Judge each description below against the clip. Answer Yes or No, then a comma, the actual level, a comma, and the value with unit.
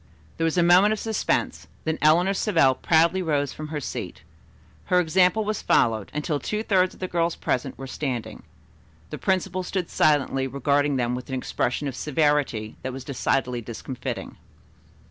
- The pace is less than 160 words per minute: No, average, 165 wpm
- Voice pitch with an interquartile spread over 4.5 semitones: Yes, average, 5.3 semitones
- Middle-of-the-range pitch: Yes, medium, 150 Hz